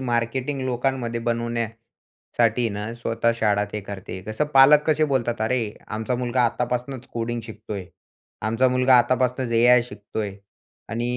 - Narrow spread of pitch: Yes, narrow, 2.2 semitones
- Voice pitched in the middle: No, low, 120 Hz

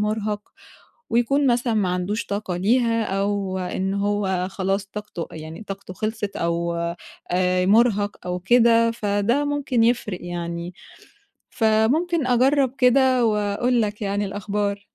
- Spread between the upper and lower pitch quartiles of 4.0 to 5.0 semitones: No, average, 3.5 semitones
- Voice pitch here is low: No, high, 205 Hz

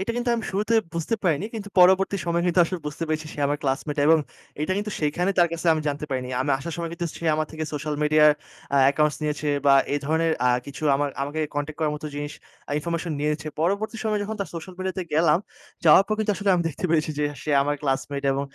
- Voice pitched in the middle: Yes, medium, 155 Hz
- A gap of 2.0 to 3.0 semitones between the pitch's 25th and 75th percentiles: No, average, 3.6 semitones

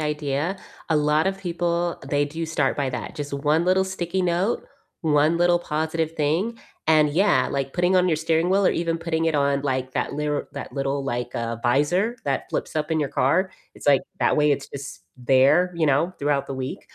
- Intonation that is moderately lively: Yes, average, 3.6 semitones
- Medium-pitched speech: Yes, medium, 155 Hz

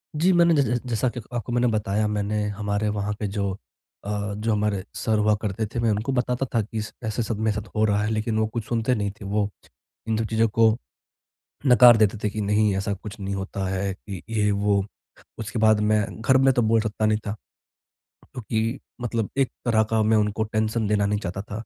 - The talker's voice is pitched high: No, low, 110 Hz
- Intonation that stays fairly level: Yes, narrow, 1.8 semitones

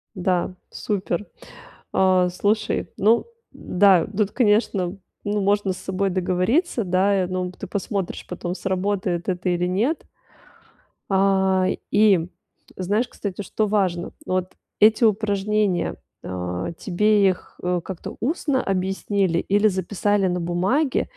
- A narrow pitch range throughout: Yes, narrow, 2.3 semitones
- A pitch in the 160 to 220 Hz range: Yes, high, 190 Hz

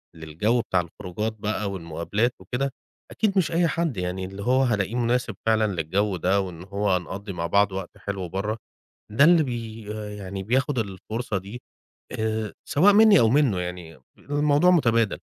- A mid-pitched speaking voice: No, low, 105 Hz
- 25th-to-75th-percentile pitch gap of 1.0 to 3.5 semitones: No, average, 4.9 semitones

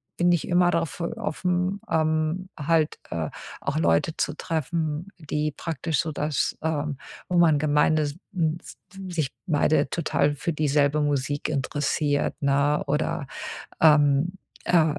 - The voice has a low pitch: No, medium, 155 Hz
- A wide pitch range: No, narrow, 2.5 semitones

